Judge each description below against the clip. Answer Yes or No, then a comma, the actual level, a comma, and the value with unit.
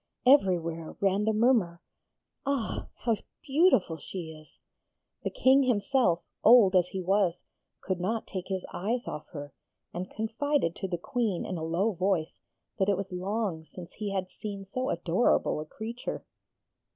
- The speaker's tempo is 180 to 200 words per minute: No, average, 155 wpm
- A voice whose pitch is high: Yes, high, 195 Hz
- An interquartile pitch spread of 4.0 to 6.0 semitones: Yes, average, 4.5 semitones